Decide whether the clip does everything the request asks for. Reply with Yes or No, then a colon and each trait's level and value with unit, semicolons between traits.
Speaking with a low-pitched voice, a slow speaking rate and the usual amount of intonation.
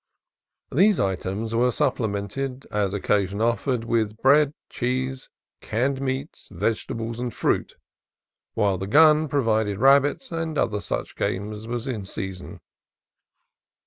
Yes: low, 115 Hz; slow, 120 wpm; average, 4.7 semitones